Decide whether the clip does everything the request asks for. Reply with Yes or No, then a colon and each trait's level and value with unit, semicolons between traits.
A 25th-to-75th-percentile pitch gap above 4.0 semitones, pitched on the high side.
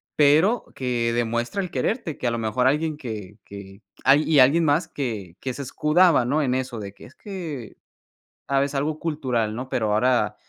No: average, 4.6 semitones; low, 130 Hz